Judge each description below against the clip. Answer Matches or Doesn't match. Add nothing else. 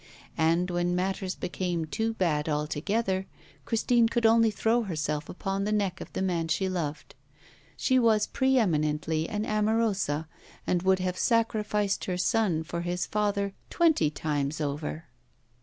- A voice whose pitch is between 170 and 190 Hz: Matches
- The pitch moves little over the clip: Doesn't match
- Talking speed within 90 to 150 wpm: Matches